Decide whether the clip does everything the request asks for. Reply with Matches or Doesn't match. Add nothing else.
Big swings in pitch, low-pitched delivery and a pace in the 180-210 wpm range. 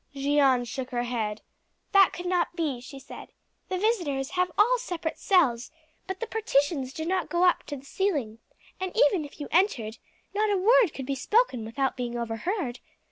Doesn't match